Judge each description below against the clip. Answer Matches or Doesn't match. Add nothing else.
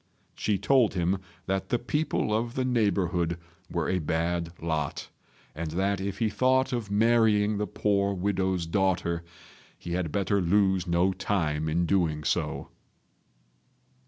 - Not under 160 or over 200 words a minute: Doesn't match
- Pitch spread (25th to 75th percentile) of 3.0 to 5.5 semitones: Matches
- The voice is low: Matches